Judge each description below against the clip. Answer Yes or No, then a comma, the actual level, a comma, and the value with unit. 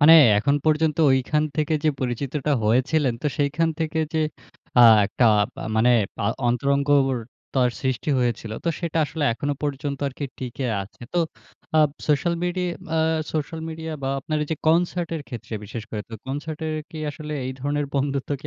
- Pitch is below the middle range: No, medium, 145 Hz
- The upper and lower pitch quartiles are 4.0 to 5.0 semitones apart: No, average, 3.4 semitones